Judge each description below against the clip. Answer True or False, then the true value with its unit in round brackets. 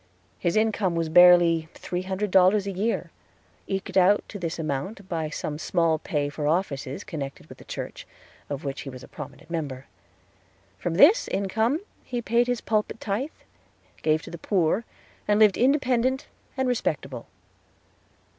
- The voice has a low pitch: False (180 Hz)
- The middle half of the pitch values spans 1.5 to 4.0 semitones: False (5.5 semitones)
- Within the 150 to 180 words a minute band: True (155 wpm)